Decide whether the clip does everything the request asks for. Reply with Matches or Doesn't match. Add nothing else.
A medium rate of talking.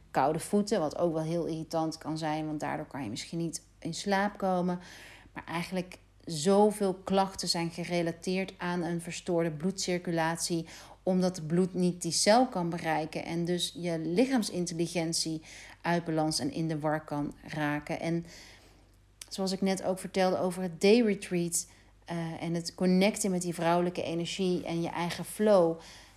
Matches